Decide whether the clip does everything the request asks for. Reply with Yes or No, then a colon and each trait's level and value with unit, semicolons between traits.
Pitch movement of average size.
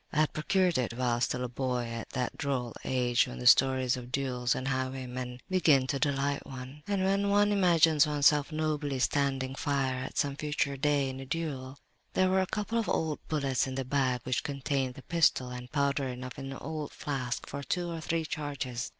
Yes: average, 3.1 semitones